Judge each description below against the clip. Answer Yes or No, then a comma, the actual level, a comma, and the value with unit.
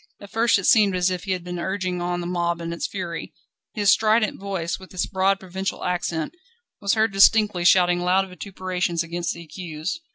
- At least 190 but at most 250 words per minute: Yes, average, 195 wpm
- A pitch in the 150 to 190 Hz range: Yes, medium, 185 Hz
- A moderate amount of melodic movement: No, narrow, 2.1 semitones